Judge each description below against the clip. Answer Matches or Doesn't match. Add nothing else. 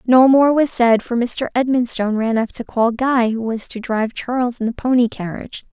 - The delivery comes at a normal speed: Doesn't match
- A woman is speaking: Matches